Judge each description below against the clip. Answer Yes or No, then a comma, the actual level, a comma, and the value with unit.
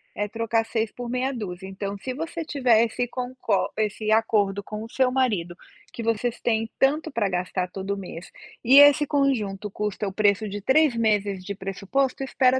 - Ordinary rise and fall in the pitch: Yes, average, 4.1 semitones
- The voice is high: Yes, high, 220 Hz